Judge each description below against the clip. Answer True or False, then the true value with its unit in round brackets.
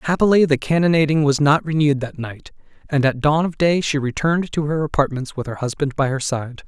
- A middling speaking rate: False (215 wpm)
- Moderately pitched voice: True (145 Hz)